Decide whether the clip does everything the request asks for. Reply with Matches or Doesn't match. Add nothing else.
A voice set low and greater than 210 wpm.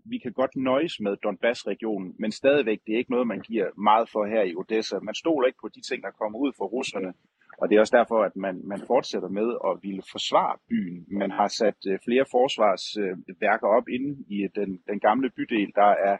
Matches